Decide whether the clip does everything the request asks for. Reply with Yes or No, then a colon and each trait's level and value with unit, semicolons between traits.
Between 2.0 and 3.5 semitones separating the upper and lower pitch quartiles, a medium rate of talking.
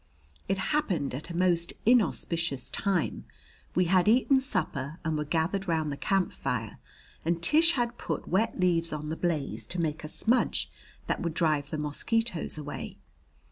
No: average, 4.2 semitones; average, 165 wpm